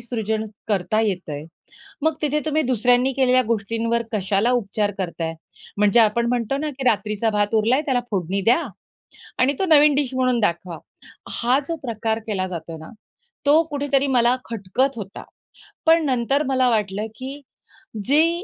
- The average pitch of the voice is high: Yes, high, 235 Hz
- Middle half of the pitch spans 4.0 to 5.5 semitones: Yes, average, 4.7 semitones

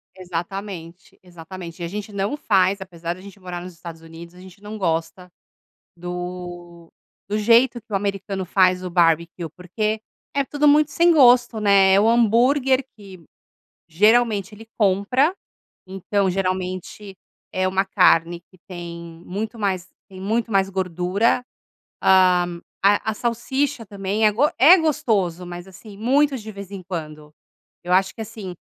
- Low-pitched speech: No, high, 190 Hz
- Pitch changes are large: No, average, 3.5 semitones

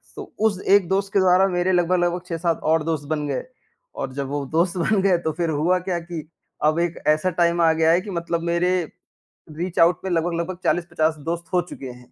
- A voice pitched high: No, medium, 170 Hz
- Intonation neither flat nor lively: No, narrow, 2.1 semitones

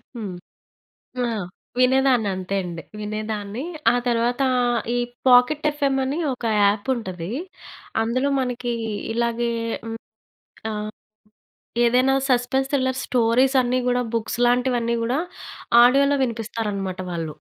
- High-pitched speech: Yes, high, 240 Hz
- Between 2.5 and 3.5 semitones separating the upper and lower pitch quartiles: Yes, average, 3.1 semitones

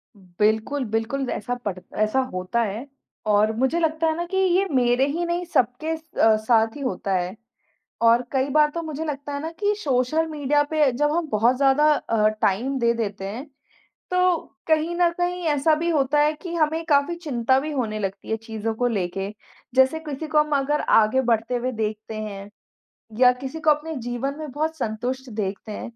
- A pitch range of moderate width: No, wide, 5.7 semitones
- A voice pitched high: Yes, very high, 265 Hz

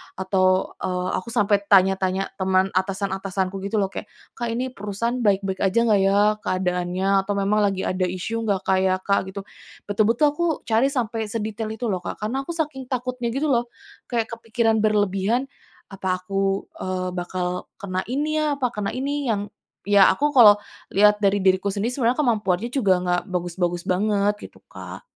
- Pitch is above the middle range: Yes, high, 205 Hz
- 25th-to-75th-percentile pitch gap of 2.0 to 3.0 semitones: No, average, 3.7 semitones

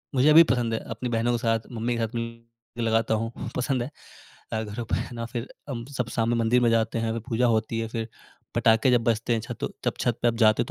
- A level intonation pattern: Yes, narrow, 1.2 semitones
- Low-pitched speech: Yes, low, 115 Hz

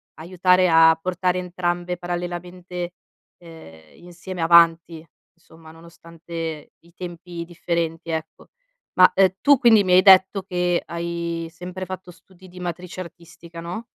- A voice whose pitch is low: No, medium, 175 Hz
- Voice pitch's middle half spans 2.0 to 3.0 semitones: No, narrow, 1.5 semitones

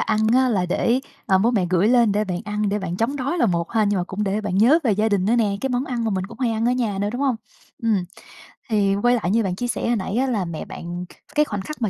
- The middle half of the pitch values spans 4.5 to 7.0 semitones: No, average, 3.8 semitones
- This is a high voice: Yes, high, 215 Hz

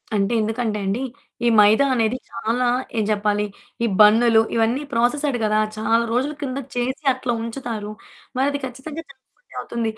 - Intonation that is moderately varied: Yes, average, 3.2 semitones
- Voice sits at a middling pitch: No, high, 235 Hz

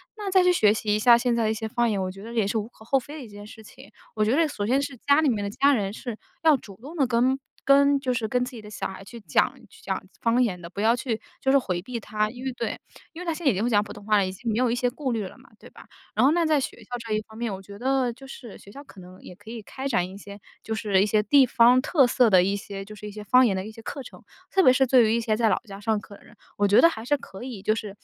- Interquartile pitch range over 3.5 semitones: Yes, average, 4.0 semitones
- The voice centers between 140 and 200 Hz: No, high, 225 Hz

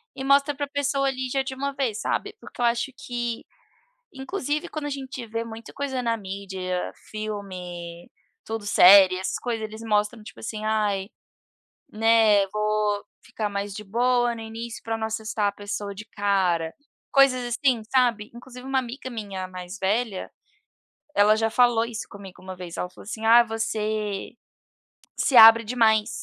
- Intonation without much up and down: No, average, 3.4 semitones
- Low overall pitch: No, high, 220 Hz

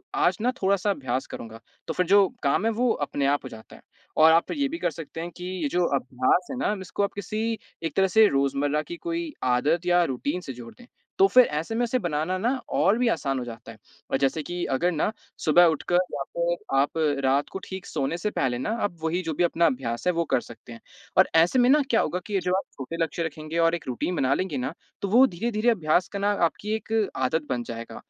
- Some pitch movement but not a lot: No, wide, 6.5 semitones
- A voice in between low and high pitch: Yes, medium, 170 Hz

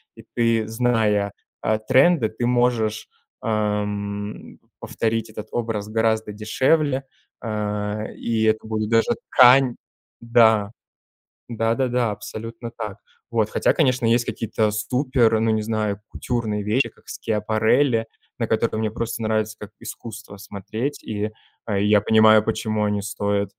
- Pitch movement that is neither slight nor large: No, narrow, 1.8 semitones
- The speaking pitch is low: Yes, low, 110 Hz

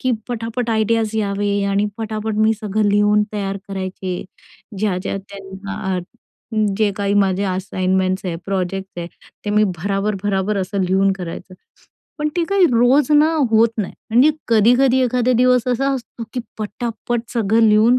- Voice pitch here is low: No, high, 210 Hz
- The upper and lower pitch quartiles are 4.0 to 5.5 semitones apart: No, average, 3.2 semitones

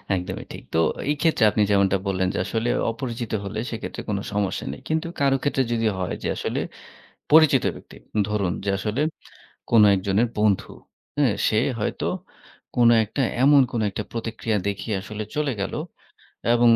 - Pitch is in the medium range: No, low, 110 Hz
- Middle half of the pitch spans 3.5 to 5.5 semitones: Yes, average, 4.4 semitones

